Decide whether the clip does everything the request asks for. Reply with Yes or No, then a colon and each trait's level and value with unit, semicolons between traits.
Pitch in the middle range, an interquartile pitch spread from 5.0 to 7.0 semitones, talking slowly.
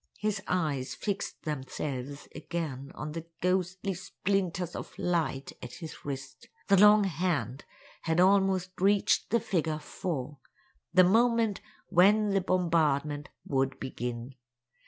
Yes: medium, 170 Hz; wide, 5.5 semitones; slow, 115 wpm